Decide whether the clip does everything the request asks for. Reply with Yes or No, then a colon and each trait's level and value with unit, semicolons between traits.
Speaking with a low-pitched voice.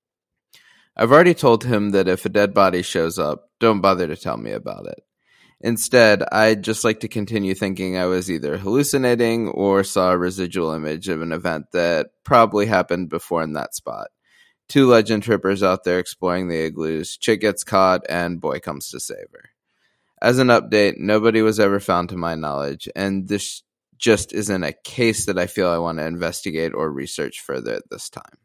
Yes: very low, 95 Hz